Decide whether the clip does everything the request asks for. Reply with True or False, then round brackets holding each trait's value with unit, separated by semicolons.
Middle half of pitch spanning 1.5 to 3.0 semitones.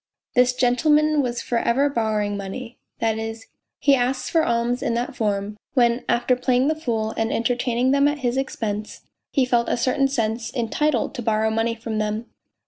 True (2.6 semitones)